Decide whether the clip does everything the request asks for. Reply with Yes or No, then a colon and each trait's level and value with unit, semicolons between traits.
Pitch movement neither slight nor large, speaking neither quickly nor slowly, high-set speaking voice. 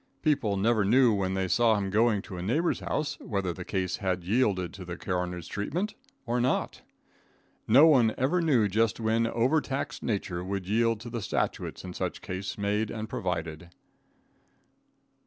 No: average, 4.3 semitones; average, 170 wpm; low, 105 Hz